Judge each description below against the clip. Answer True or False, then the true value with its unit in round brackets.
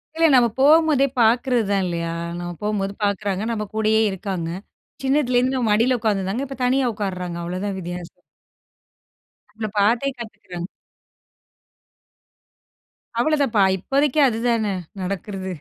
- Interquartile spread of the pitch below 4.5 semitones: False (4.8 semitones)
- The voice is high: True (215 Hz)